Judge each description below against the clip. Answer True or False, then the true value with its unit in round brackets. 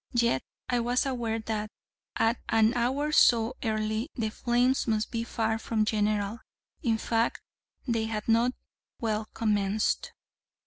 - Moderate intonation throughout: False (1.7 semitones)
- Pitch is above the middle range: True (225 Hz)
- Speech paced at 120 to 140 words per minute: True (135 wpm)